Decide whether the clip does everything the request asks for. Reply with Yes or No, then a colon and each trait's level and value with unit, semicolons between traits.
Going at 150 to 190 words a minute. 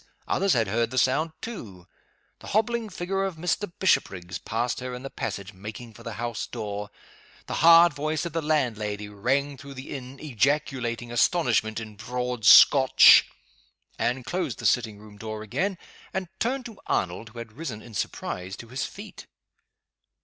Yes: average, 165 wpm